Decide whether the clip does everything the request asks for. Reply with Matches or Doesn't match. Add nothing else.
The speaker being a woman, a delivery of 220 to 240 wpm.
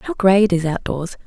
Matches